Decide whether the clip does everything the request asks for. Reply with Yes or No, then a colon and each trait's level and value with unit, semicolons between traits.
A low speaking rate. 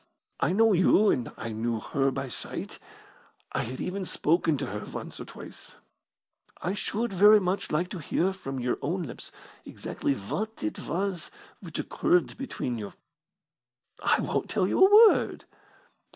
No: average, 160 wpm